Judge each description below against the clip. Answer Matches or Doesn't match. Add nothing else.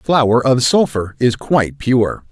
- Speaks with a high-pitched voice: Doesn't match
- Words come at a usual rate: Matches